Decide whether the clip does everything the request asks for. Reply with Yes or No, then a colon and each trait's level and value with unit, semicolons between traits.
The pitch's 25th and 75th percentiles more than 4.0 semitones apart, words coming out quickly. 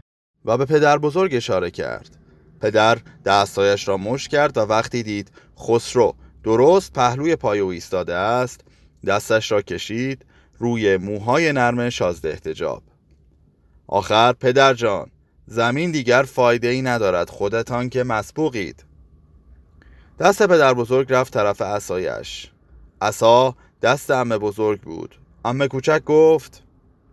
No: average, 4.9 semitones; average, 120 wpm